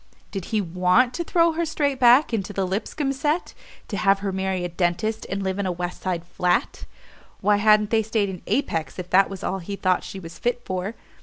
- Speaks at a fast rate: Yes, fast, 220 wpm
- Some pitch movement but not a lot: Yes, average, 4.1 semitones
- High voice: Yes, high, 195 Hz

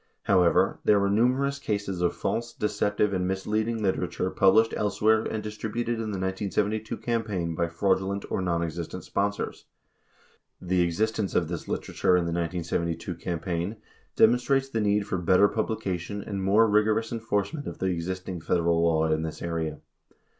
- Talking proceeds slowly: No, average, 160 wpm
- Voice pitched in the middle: No, low, 100 Hz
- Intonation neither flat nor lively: Yes, average, 3.9 semitones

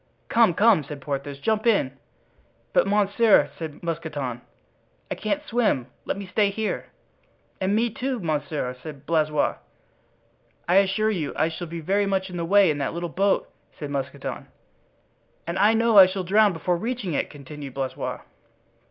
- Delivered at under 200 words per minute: Yes, average, 160 wpm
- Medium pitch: Yes, medium, 180 Hz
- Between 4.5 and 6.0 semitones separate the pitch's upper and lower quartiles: Yes, wide, 5.6 semitones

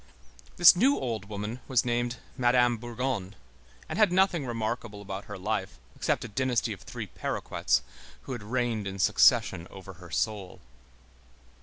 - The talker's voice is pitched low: Yes, low, 115 Hz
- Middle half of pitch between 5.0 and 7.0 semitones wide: No, average, 3.7 semitones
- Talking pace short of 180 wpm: Yes, average, 150 wpm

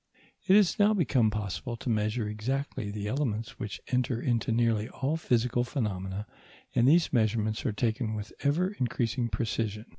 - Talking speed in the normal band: Yes, average, 155 wpm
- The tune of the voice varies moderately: Yes, average, 3.6 semitones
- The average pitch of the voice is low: Yes, low, 115 Hz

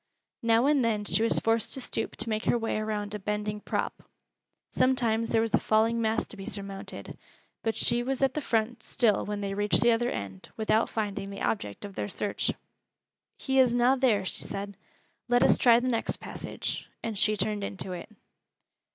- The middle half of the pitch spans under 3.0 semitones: Yes, narrow, 2.4 semitones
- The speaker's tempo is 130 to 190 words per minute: No, average, 200 wpm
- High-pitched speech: Yes, high, 220 Hz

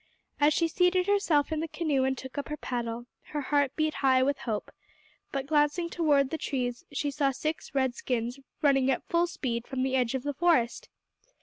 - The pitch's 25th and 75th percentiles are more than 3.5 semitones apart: No, average, 3.1 semitones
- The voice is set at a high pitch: Yes, very high, 280 Hz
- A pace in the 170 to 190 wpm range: No, average, 200 wpm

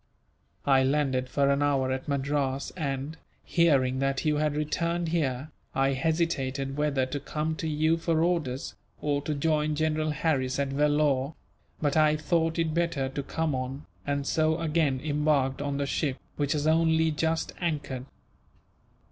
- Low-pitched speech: No, medium, 150 Hz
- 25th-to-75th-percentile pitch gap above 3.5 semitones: No, narrow, 2.6 semitones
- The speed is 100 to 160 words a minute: Yes, average, 155 wpm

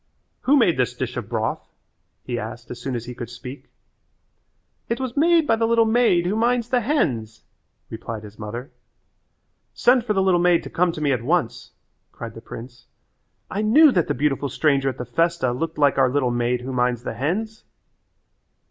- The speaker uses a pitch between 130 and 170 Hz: Yes, medium, 140 Hz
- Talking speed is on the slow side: No, average, 190 wpm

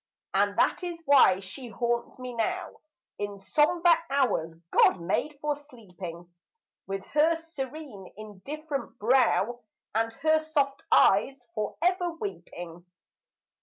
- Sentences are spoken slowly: Yes, slow, 120 wpm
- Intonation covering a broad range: Yes, wide, 7.3 semitones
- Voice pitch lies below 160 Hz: No, very high, 255 Hz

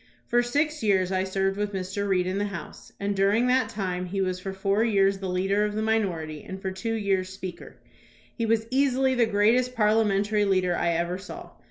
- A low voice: No, high, 200 Hz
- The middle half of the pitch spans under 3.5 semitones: Yes, average, 2.8 semitones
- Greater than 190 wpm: Yes, fast, 205 wpm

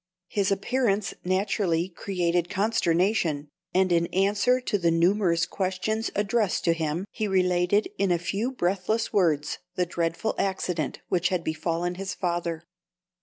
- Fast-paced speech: No, slow, 135 wpm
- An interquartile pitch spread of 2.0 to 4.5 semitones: Yes, average, 2.9 semitones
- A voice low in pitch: No, medium, 185 Hz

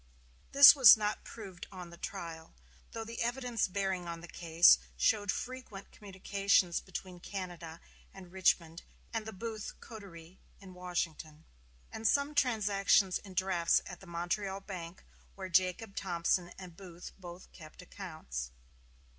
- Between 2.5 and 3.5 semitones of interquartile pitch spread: Yes, average, 3.1 semitones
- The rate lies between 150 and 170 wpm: No, average, 140 wpm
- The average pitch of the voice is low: No, medium, 185 Hz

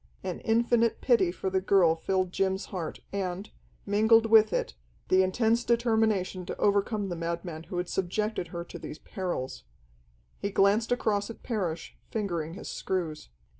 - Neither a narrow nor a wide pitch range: Yes, average, 3.7 semitones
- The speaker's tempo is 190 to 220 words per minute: No, average, 155 wpm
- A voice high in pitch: Yes, high, 195 Hz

